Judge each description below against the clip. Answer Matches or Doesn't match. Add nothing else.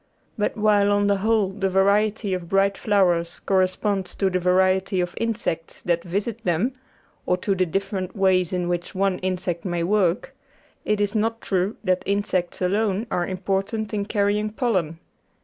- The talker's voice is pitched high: Matches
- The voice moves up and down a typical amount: Doesn't match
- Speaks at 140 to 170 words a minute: Matches